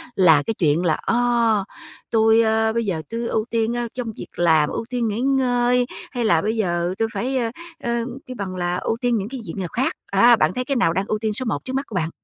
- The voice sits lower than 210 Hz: No, high, 225 Hz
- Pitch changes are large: No, average, 4.6 semitones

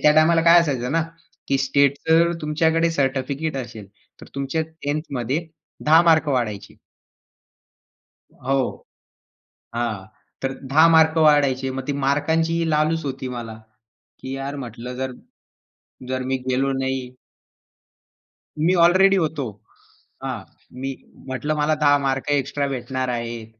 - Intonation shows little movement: No, average, 3.5 semitones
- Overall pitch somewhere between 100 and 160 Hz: Yes, medium, 140 Hz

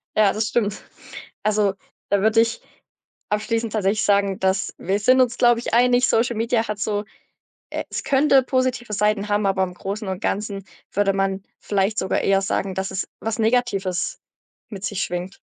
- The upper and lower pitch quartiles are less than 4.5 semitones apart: Yes, average, 2.8 semitones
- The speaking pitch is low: No, high, 210 Hz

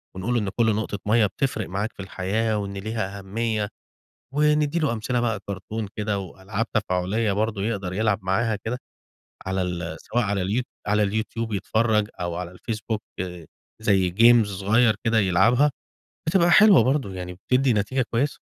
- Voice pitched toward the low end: Yes, low, 105 Hz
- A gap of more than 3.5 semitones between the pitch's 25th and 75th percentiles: No, average, 3.1 semitones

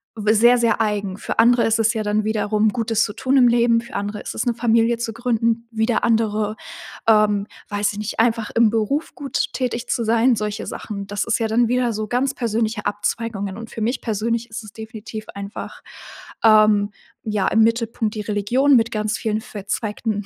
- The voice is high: Yes, high, 220 Hz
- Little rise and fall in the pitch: Yes, narrow, 1.8 semitones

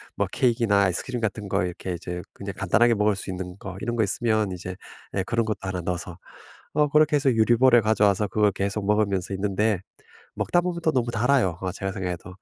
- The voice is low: Yes, low, 105 Hz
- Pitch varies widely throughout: No, average, 3.9 semitones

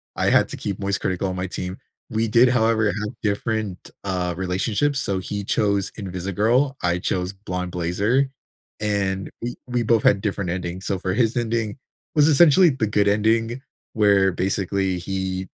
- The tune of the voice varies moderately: Yes, average, 3.3 semitones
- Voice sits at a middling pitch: No, low, 100 Hz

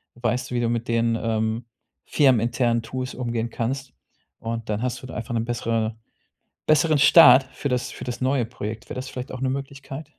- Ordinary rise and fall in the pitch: No, narrow, 2.2 semitones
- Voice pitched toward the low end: Yes, low, 120 Hz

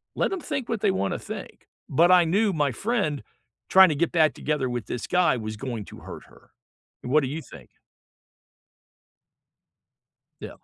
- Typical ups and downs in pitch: No, wide, 6.7 semitones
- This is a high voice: No, medium, 155 Hz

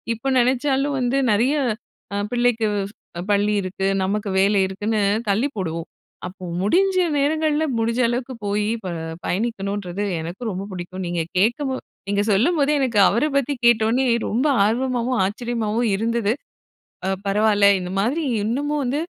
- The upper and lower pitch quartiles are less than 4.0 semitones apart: No, average, 4.3 semitones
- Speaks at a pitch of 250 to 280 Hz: No, high, 225 Hz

